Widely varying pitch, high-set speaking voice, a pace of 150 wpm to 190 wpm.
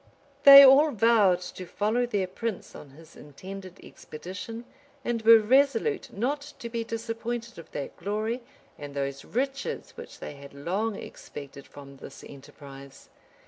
No: wide, 8.1 semitones; high, 215 Hz; average, 140 wpm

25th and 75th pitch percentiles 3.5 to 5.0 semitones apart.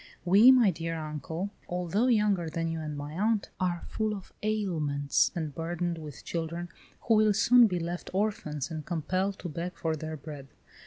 Yes: average, 4.2 semitones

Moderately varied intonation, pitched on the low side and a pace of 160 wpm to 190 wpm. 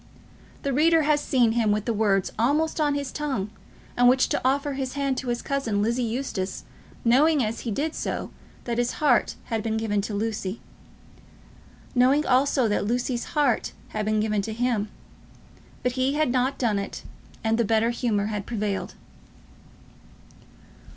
No: average, 4.0 semitones; high, 240 Hz; average, 165 wpm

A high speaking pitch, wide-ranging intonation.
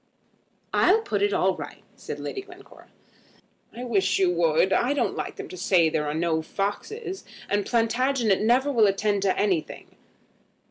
Yes: high, 215 Hz; wide, 7.3 semitones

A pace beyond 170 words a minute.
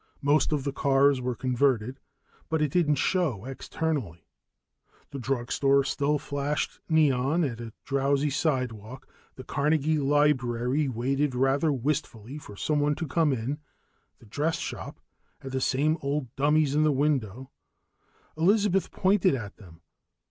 No: average, 140 wpm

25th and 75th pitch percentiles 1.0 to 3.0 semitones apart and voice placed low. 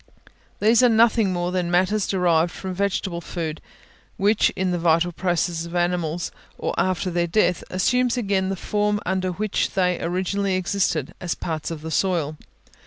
No: narrow, 2.5 semitones; medium, 180 Hz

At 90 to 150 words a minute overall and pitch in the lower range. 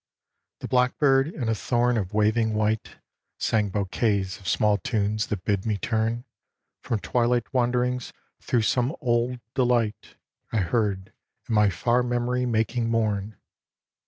Yes: average, 140 wpm; low, 115 Hz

